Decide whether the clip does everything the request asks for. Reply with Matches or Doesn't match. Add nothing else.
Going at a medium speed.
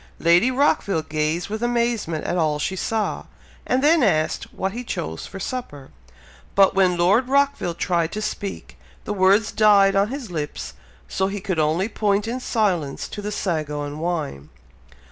Matches